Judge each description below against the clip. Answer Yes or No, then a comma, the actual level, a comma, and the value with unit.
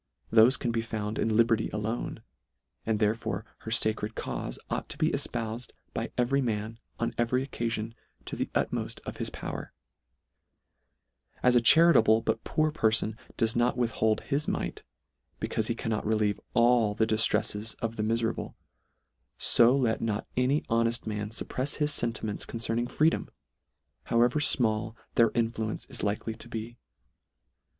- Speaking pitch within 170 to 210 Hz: No, low, 115 Hz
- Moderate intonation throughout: No, narrow, 1.6 semitones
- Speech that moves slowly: No, average, 150 wpm